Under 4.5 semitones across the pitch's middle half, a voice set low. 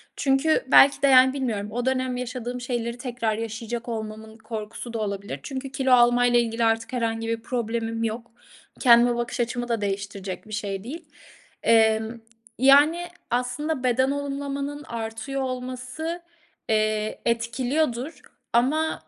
No: narrow, 2.6 semitones; high, 240 Hz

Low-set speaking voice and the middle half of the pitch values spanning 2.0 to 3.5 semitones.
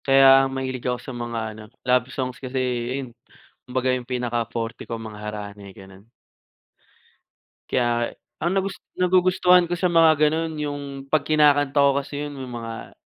No: low, 130 Hz; average, 4.1 semitones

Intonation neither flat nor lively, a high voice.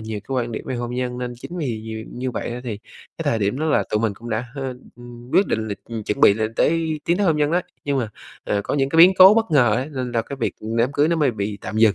No: average, 4.8 semitones; low, 120 Hz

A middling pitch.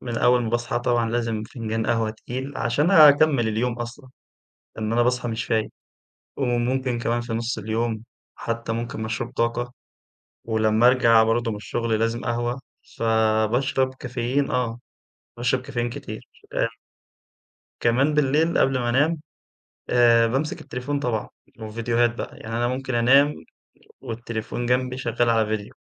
No: low, 120 Hz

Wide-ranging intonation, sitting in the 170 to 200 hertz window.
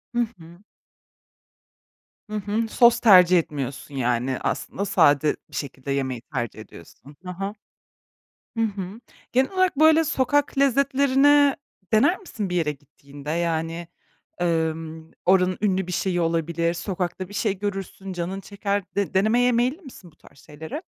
Yes: wide, 6.2 semitones; medium, 185 Hz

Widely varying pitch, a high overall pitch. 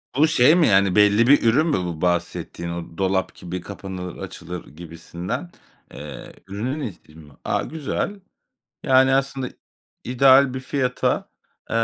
No: wide, 7.2 semitones; low, 105 Hz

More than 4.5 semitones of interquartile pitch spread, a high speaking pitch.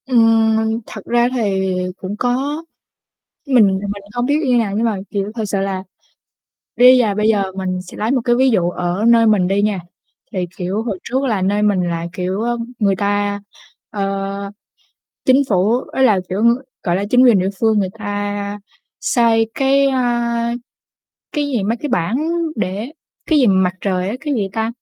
No: average, 3.5 semitones; high, 215 Hz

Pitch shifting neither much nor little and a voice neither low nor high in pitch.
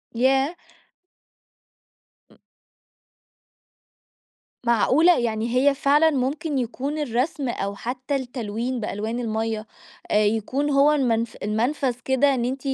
No: average, 3.5 semitones; very high, 255 Hz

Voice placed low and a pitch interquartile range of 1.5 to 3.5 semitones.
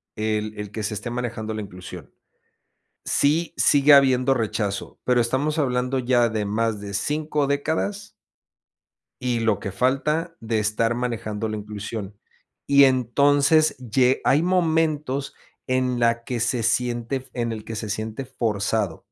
No: low, 120 Hz; average, 4.2 semitones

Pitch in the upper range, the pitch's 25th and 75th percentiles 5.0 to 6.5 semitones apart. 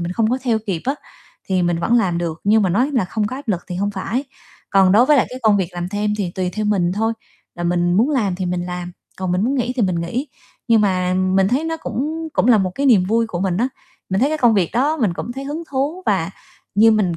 Yes: high, 205 Hz; wide, 5.4 semitones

